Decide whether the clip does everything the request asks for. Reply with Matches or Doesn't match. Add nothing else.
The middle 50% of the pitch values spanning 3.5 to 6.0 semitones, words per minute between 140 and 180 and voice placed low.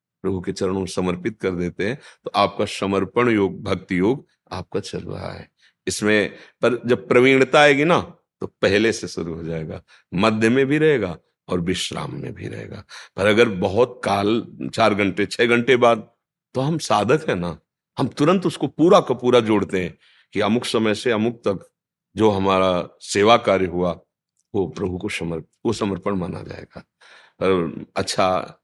Matches